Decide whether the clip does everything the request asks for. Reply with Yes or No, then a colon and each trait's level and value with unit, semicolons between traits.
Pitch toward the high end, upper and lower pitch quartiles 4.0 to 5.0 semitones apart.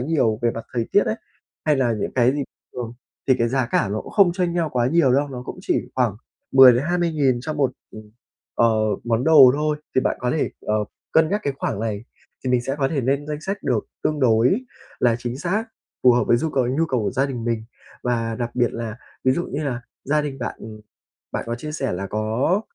No: low, 130 Hz; average, 4.3 semitones